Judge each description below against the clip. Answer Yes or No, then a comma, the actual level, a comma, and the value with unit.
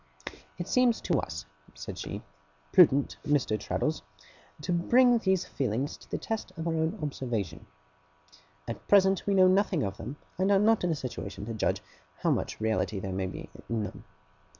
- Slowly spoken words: No, average, 175 wpm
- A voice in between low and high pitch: Yes, medium, 150 Hz